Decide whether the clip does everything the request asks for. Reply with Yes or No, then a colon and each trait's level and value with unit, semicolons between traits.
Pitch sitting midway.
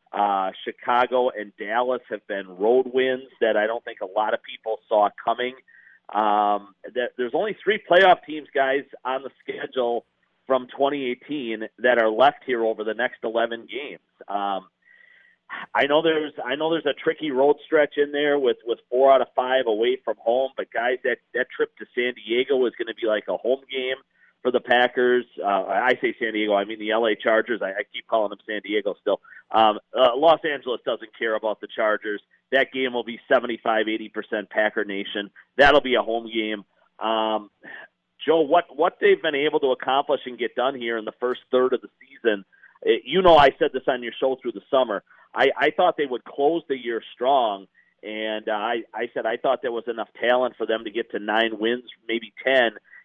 No: low, 125 Hz